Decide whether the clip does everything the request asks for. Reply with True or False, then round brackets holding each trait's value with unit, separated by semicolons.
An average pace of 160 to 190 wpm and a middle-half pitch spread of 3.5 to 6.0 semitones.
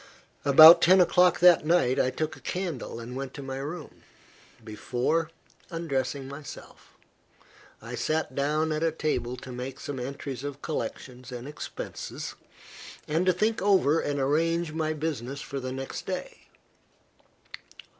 False (145 wpm; 3.8 semitones)